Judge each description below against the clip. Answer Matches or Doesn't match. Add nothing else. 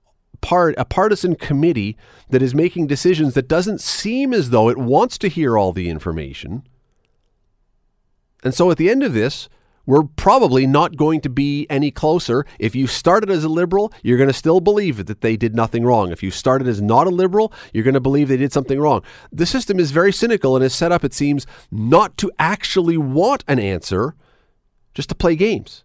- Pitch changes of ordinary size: Doesn't match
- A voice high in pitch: Doesn't match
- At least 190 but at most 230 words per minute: Matches